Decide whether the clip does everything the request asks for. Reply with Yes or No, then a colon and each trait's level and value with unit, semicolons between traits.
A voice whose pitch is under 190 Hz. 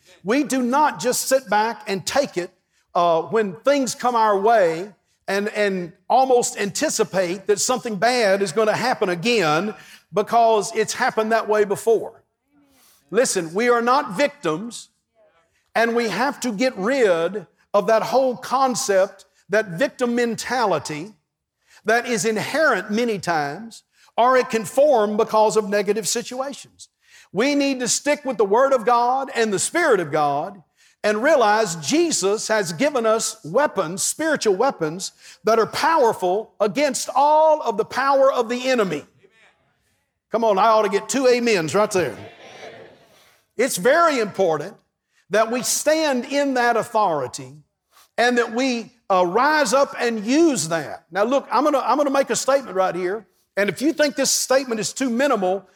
No: high, 225 Hz